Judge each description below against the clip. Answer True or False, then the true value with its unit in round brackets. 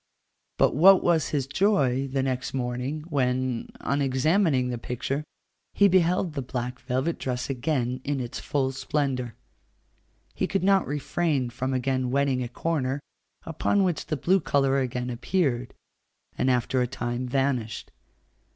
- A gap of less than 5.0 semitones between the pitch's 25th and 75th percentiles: True (3.3 semitones)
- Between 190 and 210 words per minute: False (145 wpm)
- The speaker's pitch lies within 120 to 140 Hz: True (135 Hz)